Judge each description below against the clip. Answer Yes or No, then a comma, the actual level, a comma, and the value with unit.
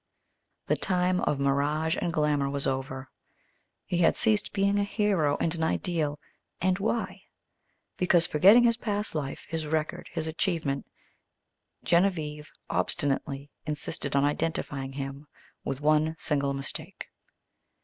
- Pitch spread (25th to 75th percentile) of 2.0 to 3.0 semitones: No, average, 4.1 semitones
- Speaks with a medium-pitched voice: Yes, medium, 155 Hz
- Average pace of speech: No, slow, 130 wpm